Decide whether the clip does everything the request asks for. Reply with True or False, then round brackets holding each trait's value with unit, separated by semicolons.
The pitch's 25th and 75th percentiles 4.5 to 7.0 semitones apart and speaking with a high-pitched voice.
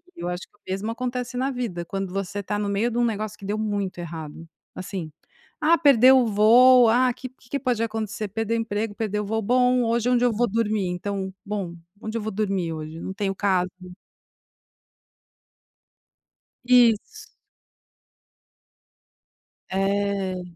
False (3.7 semitones; 210 Hz)